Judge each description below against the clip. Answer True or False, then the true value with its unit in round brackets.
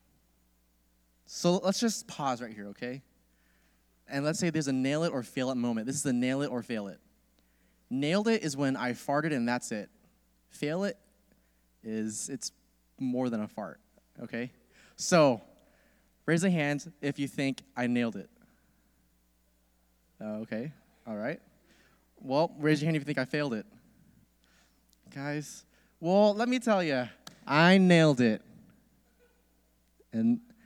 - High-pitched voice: False (125 Hz)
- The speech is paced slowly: False (150 wpm)